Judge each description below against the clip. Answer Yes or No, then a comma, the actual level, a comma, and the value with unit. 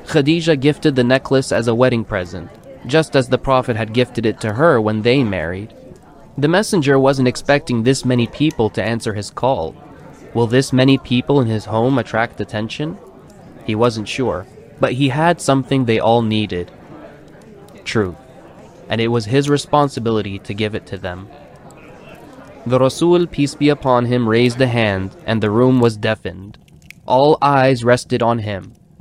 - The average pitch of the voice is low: Yes, low, 125 Hz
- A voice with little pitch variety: No, average, 3.7 semitones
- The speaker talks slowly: No, average, 165 wpm